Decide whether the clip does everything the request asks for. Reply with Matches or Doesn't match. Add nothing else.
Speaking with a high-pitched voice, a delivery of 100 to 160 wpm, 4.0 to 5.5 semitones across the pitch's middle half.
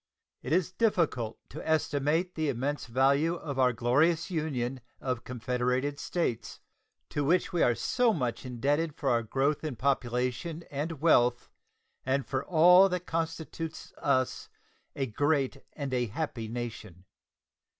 Doesn't match